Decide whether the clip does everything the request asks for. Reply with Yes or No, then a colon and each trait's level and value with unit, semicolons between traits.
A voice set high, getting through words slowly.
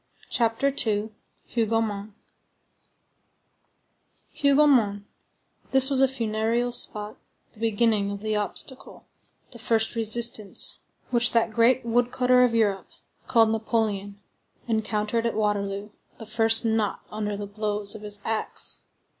Yes: high, 225 Hz; slow, 115 wpm